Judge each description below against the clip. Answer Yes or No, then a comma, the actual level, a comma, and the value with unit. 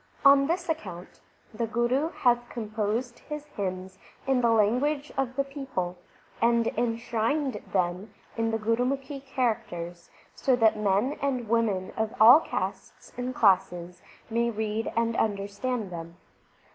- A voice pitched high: Yes, high, 230 Hz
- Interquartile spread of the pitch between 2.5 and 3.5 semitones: No, average, 4.1 semitones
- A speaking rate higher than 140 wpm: No, slow, 135 wpm